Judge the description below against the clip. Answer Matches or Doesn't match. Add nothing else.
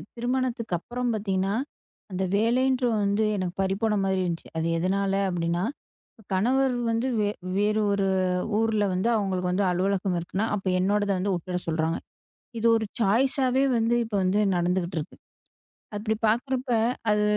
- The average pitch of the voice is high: Matches